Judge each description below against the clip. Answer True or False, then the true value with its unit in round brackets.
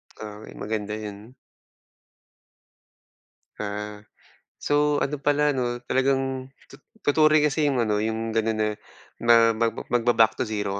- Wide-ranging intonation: False (4.0 semitones)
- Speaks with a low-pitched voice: True (115 Hz)